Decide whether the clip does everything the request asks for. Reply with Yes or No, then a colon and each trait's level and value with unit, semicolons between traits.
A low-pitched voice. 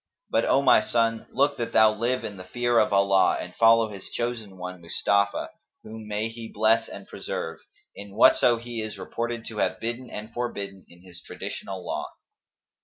Yes: low, 110 Hz